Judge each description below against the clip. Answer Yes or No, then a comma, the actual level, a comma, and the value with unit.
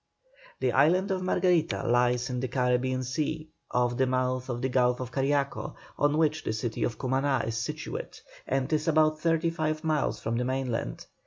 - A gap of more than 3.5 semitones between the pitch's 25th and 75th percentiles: Yes, average, 3.9 semitones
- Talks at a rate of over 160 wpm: Yes, average, 180 wpm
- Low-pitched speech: Yes, low, 130 Hz